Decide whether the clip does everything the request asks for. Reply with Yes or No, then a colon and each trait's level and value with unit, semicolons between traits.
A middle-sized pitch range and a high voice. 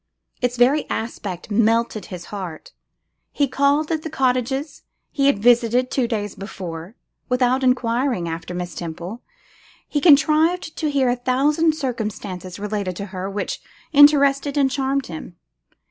No: wide, 5.8 semitones; high, 245 Hz